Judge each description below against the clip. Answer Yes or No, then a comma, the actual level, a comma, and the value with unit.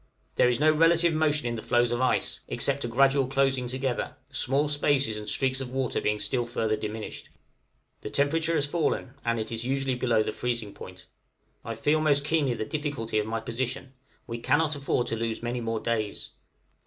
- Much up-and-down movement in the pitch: No, average, 3.6 semitones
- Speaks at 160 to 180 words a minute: No, average, 190 wpm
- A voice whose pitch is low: Yes, low, 130 Hz